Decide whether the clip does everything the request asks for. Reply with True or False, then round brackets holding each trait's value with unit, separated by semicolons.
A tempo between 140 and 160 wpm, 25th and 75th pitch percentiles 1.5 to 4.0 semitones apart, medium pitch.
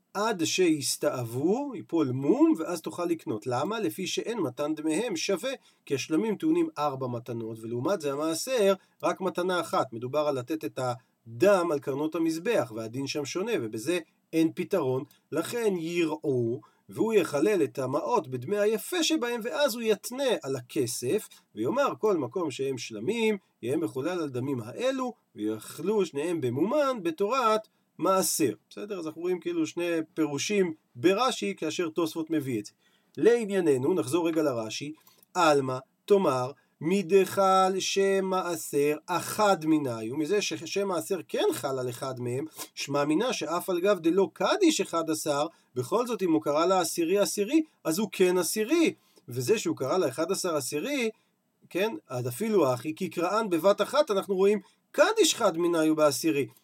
False (150 wpm; 5.4 semitones; 170 Hz)